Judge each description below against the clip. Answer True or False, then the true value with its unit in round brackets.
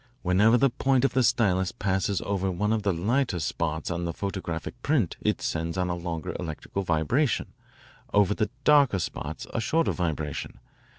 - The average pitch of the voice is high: False (95 Hz)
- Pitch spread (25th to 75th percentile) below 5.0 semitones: False (5.3 semitones)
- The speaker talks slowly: False (170 wpm)